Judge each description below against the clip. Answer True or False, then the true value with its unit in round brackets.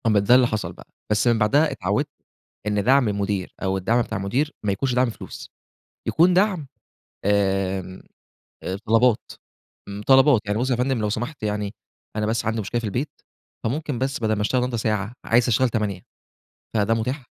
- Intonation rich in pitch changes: False (3.8 semitones)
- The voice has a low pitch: True (110 Hz)